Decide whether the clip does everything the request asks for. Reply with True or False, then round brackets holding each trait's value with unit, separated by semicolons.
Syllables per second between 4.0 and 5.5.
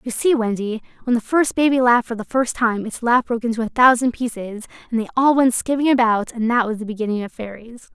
False (6.0 syllables/s)